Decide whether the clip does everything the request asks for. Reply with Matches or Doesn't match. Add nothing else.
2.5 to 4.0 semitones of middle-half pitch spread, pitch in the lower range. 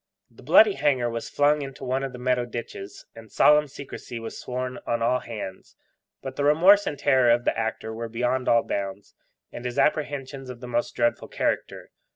Matches